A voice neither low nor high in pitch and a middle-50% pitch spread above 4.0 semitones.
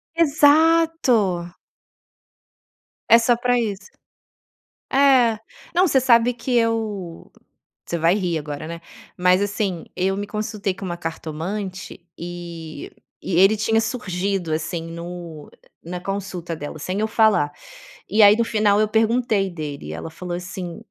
No: high, 195 Hz; average, 4.8 semitones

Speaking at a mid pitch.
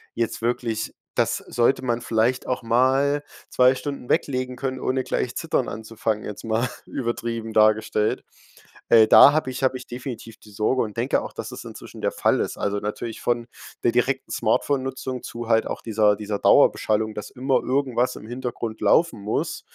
No: low, 120 Hz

